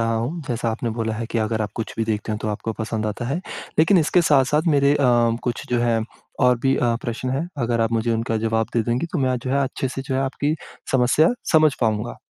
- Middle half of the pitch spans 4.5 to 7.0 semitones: No, average, 3.3 semitones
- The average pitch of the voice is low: Yes, low, 120 Hz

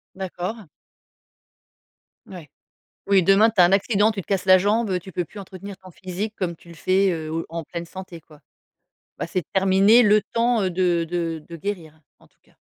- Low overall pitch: No, medium, 185 Hz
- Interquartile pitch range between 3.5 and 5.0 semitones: No, average, 2.8 semitones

